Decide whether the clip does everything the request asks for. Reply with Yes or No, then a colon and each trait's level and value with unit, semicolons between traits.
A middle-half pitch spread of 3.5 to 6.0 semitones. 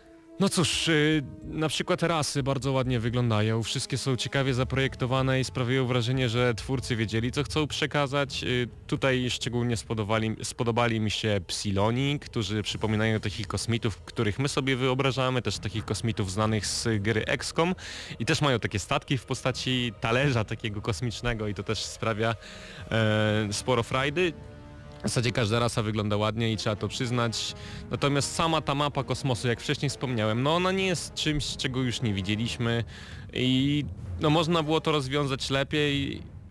Yes: average, 4.2 semitones